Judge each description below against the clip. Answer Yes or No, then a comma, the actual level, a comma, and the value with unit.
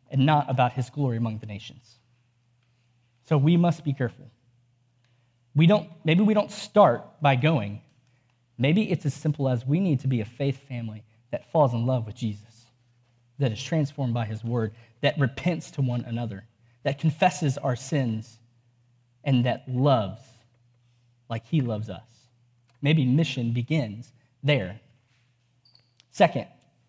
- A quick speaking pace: No, average, 145 wpm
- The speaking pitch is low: Yes, low, 125 Hz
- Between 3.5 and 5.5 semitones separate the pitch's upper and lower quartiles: No, average, 3.0 semitones